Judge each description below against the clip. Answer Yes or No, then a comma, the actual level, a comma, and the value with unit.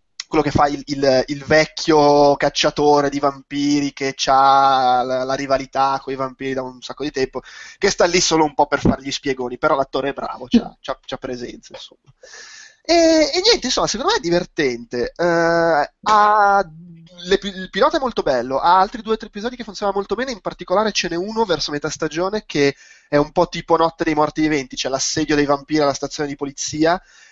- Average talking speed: No, fast, 205 wpm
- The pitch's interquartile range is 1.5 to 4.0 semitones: No, average, 5.1 semitones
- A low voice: No, medium, 155 Hz